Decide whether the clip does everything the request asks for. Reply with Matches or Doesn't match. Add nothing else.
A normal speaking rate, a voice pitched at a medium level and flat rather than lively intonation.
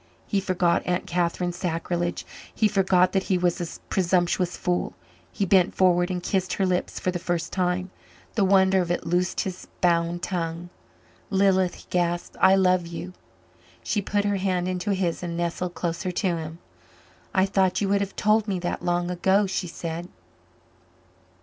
Matches